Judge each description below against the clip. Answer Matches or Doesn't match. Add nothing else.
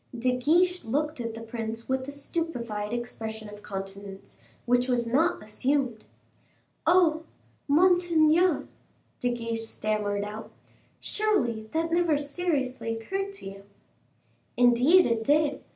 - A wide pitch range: Matches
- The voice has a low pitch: Doesn't match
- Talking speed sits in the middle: Doesn't match